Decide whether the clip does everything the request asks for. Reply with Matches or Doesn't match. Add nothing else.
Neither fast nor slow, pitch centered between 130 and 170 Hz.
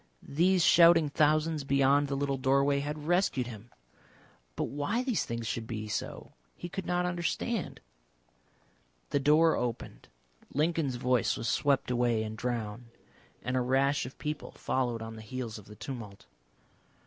Matches